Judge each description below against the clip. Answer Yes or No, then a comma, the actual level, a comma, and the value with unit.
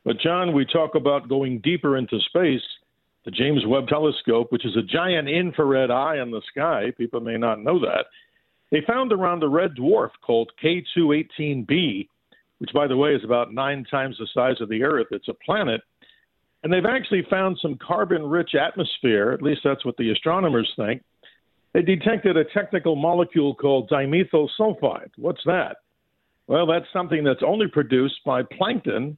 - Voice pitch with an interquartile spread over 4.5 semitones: Yes, average, 5.0 semitones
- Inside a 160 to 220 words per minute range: Yes, average, 175 wpm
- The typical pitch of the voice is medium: Yes, medium, 150 Hz